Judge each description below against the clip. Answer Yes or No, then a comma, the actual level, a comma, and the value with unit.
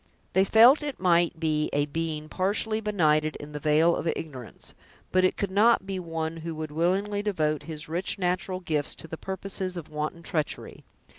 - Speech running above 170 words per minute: Yes, average, 180 wpm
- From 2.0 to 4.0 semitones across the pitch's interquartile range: Yes, average, 3.7 semitones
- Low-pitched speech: No, medium, 170 Hz